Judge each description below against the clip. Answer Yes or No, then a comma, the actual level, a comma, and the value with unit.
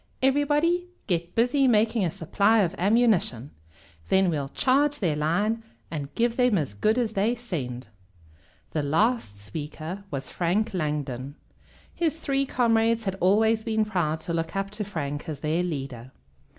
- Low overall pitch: No, high, 195 Hz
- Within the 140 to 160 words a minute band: Yes, average, 150 wpm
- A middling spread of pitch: No, wide, 7.0 semitones